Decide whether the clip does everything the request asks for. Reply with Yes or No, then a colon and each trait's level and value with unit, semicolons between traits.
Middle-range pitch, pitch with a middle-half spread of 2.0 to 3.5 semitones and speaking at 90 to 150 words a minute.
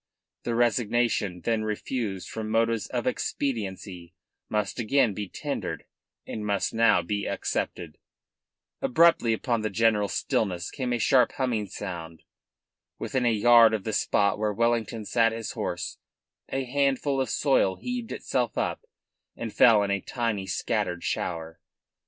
No: low, 110 Hz; average, 3.1 semitones; average, 140 wpm